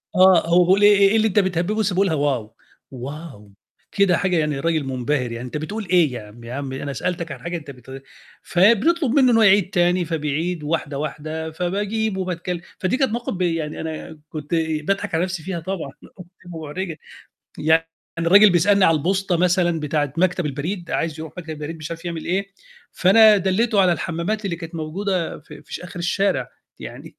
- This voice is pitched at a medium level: Yes, medium, 170 Hz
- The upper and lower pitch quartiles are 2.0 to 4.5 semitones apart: Yes, average, 3.8 semitones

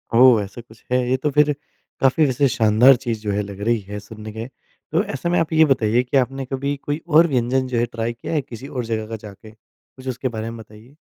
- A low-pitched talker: Yes, low, 125 Hz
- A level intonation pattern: No, average, 3.5 semitones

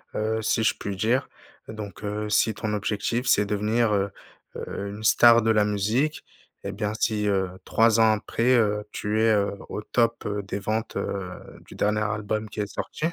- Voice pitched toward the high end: No, low, 105 Hz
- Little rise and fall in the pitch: Yes, narrow, 1.5 semitones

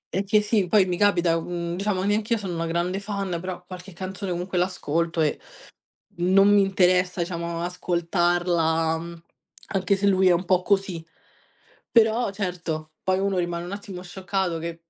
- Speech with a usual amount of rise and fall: No, narrow, 2.3 semitones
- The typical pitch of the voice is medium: Yes, medium, 180 Hz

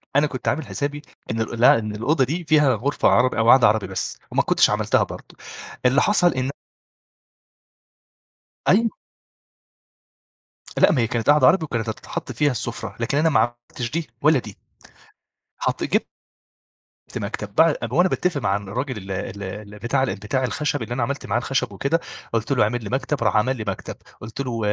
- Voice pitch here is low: Yes, low, 125 Hz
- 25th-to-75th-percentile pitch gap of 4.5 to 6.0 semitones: Yes, average, 4.8 semitones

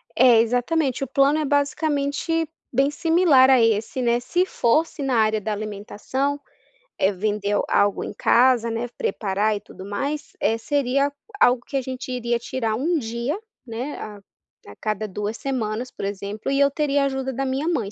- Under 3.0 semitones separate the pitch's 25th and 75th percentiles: No, average, 4.5 semitones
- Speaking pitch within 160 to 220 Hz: No, very high, 250 Hz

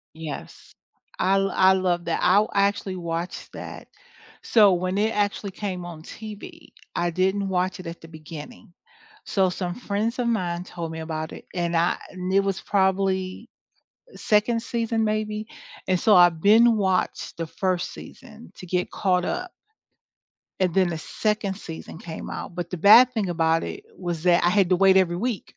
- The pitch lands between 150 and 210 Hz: Yes, medium, 185 Hz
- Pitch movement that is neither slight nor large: Yes, average, 3.1 semitones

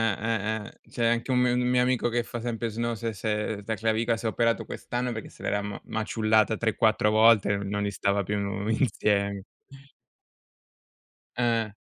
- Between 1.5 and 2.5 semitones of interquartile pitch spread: Yes, narrow, 2.1 semitones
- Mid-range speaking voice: No, low, 110 Hz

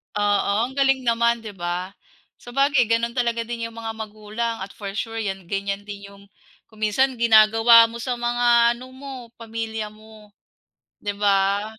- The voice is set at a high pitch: Yes, high, 225 Hz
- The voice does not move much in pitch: Yes, narrow, 2.3 semitones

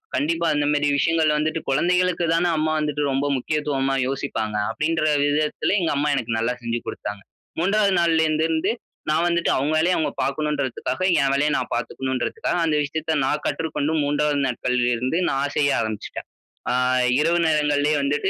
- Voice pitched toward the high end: No, medium, 150 Hz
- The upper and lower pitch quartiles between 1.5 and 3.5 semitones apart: Yes, average, 2.8 semitones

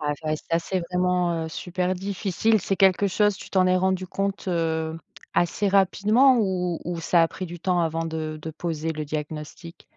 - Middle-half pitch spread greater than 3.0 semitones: No, average, 2.7 semitones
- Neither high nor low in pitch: Yes, medium, 180 Hz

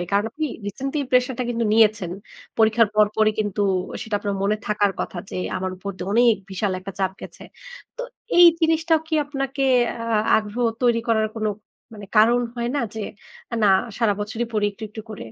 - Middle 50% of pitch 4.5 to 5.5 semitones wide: No, average, 3.0 semitones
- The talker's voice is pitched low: No, high, 220 Hz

